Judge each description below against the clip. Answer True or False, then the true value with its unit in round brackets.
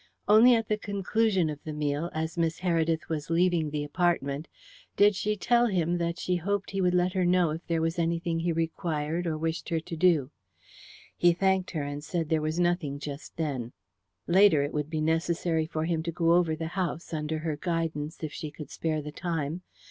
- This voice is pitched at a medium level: True (165 Hz)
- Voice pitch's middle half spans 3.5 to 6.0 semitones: False (2.4 semitones)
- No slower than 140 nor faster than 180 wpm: False (205 wpm)